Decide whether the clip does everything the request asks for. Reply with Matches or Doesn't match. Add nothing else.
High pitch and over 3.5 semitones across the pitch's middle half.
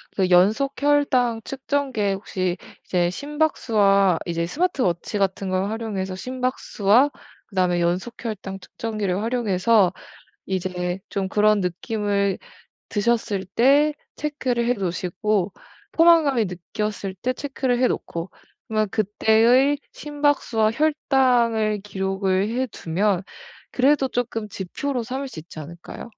Matches